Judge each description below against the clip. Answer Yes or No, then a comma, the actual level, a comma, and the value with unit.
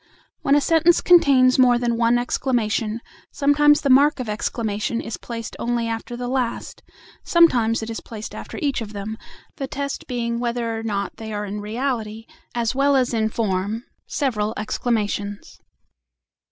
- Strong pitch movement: No, average, 3.2 semitones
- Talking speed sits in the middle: Yes, average, 160 wpm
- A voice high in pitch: Yes, high, 235 Hz